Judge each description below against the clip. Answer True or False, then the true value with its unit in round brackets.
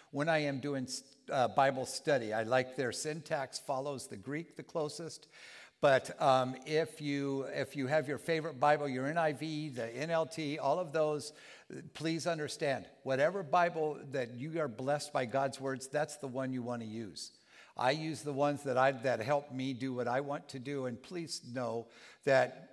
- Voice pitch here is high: False (140 Hz)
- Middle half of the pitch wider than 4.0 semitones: False (2.9 semitones)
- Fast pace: False (185 wpm)